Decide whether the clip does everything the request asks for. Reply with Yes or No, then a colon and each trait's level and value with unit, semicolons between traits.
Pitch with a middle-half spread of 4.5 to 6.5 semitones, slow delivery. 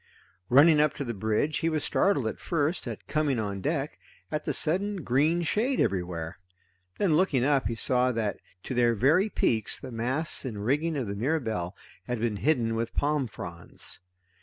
No: wide, 5.5 semitones; average, 180 wpm